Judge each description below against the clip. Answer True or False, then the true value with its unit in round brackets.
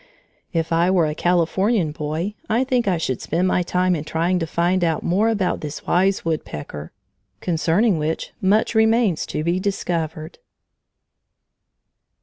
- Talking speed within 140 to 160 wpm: True (145 wpm)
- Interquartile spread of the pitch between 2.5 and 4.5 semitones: True (3.2 semitones)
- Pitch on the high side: False (175 Hz)